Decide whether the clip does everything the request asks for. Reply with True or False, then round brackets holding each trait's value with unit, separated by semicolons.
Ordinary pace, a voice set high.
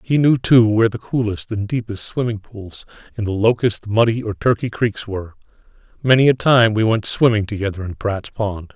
False (190 wpm; 110 Hz)